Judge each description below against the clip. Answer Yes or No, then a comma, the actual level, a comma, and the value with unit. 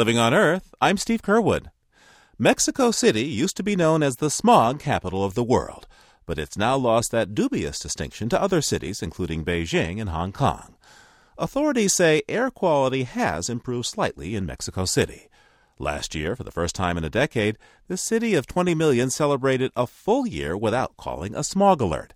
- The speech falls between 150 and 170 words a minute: No, average, 180 wpm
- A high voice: No, low, 135 Hz